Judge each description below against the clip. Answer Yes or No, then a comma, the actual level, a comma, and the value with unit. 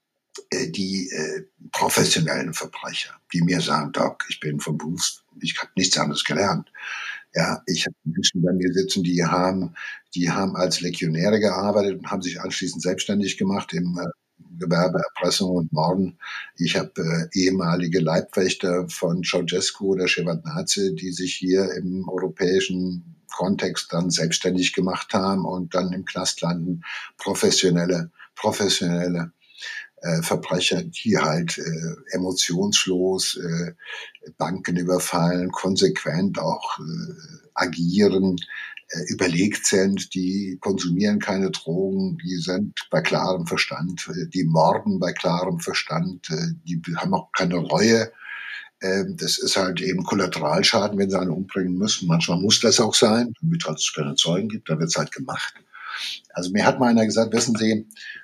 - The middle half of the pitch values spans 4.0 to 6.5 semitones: No, narrow, 2.4 semitones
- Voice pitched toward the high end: No, very low, 90 Hz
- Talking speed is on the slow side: No, average, 140 wpm